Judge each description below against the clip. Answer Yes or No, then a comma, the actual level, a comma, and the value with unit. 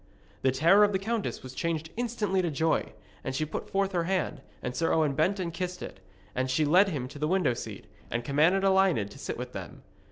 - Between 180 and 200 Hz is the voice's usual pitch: No, medium, 165 Hz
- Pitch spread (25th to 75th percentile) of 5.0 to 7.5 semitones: Yes, average, 5.3 semitones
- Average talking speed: No, fast, 225 wpm